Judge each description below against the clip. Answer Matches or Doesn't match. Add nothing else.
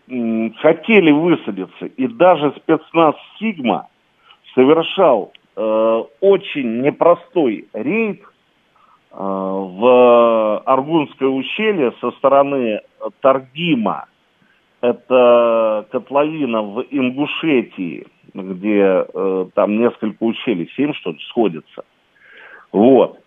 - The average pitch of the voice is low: Matches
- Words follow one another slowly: Matches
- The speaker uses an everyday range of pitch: Doesn't match